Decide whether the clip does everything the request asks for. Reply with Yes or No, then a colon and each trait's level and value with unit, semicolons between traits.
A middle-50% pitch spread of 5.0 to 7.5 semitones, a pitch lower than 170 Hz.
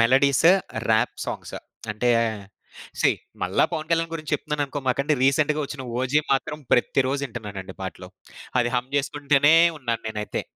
No: average, 3.9 semitones; low, 135 Hz